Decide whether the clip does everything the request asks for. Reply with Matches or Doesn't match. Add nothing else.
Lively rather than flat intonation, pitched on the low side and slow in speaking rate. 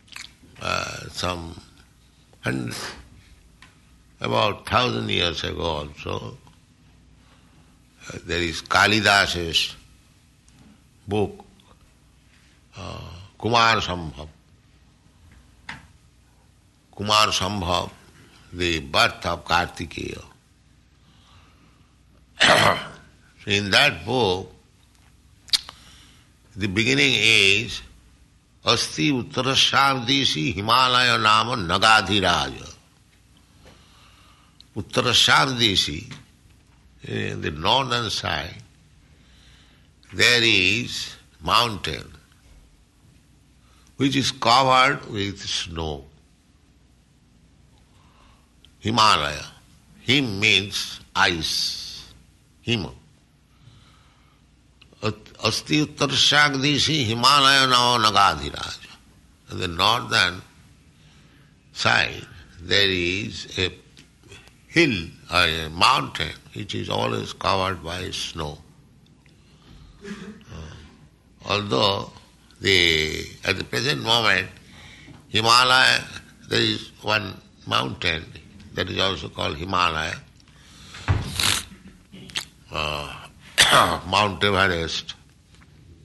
Matches